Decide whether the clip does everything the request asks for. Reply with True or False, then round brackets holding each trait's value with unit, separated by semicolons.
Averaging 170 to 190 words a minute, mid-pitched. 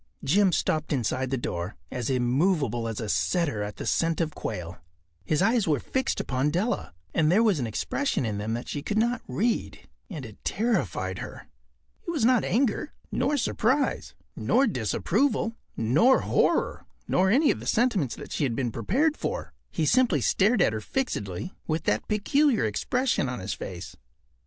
True (175 wpm; 160 Hz)